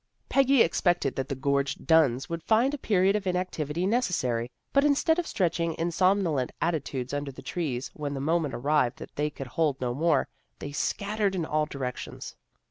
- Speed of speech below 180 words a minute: No, average, 185 wpm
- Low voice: No, medium, 160 Hz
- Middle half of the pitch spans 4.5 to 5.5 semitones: Yes, average, 5.2 semitones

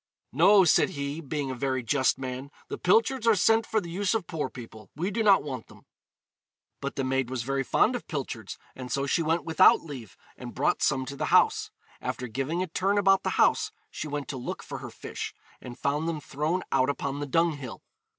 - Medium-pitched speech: Yes, medium, 145 Hz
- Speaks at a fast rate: Yes, fast, 215 wpm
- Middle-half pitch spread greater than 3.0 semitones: Yes, wide, 5.4 semitones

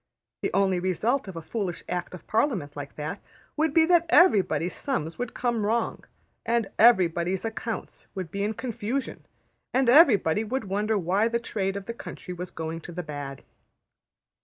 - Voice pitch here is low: No, high, 200 Hz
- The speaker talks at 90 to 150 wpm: No, average, 165 wpm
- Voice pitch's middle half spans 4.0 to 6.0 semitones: Yes, average, 5.0 semitones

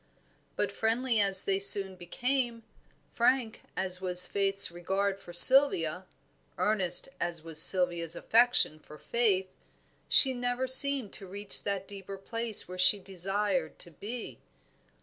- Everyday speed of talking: No, slow, 130 wpm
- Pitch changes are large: No, average, 4.2 semitones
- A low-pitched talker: No, high, 195 Hz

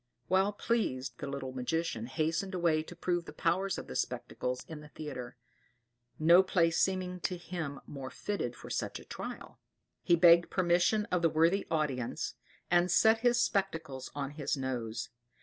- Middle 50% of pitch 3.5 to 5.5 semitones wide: Yes, average, 4.8 semitones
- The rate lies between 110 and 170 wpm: Yes, average, 165 wpm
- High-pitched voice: No, medium, 165 Hz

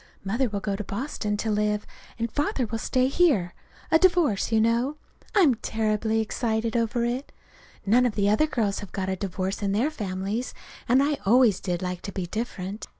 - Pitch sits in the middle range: No, high, 220 Hz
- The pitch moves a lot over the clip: No, average, 3.8 semitones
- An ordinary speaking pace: Yes, average, 190 wpm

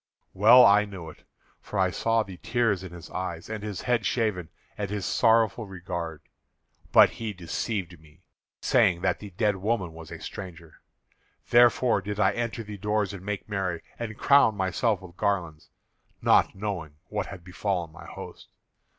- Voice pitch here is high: No, low, 100 Hz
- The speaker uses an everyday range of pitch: Yes, average, 3.4 semitones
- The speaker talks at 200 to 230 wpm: No, average, 165 wpm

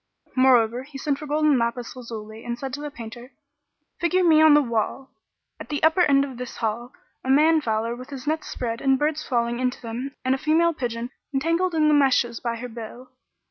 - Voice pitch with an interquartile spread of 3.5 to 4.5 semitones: Yes, average, 4.0 semitones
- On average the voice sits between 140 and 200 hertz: No, very high, 260 Hz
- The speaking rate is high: Yes, fast, 215 wpm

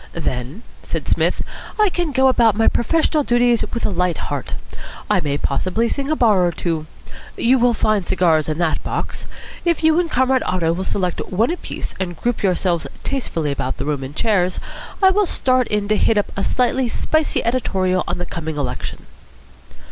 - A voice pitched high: Yes, high, 205 Hz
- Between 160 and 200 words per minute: Yes, average, 185 wpm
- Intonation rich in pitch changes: Yes, wide, 7.0 semitones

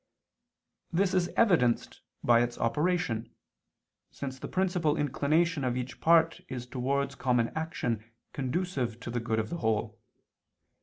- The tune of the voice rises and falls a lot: Yes, wide, 5.8 semitones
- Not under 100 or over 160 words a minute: Yes, slow, 135 wpm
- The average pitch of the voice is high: No, low, 135 Hz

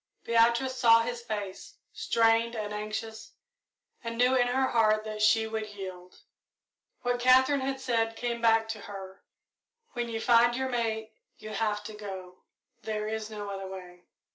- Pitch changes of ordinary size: No, narrow, 2.0 semitones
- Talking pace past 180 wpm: No, average, 160 wpm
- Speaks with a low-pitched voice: No, high, 225 Hz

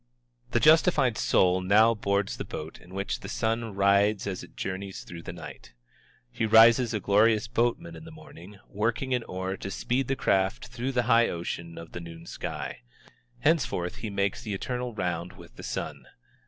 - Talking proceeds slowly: No, average, 180 wpm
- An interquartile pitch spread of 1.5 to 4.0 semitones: No, average, 4.4 semitones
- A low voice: Yes, low, 105 Hz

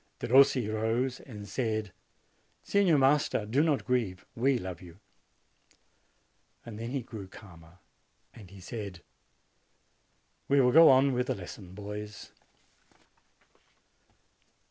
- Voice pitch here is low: Yes, low, 115 Hz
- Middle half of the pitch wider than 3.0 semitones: Yes, average, 4.7 semitones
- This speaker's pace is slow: Yes, slow, 105 wpm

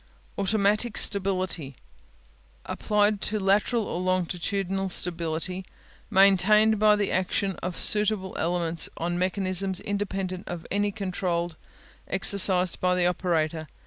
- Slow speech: Yes, slow, 110 wpm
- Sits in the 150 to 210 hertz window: Yes, high, 190 Hz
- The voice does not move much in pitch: Yes, narrow, 2.2 semitones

